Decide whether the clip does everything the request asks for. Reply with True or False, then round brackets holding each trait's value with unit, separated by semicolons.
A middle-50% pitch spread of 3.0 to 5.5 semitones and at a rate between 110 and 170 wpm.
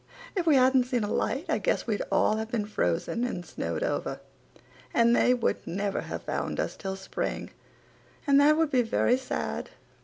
False (3.9 semitones; 185 wpm)